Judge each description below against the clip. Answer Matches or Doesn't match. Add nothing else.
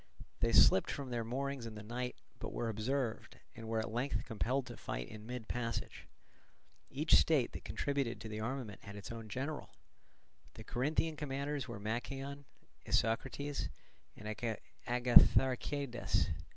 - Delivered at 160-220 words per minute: Doesn't match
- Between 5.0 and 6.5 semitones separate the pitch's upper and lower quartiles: Doesn't match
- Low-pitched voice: Matches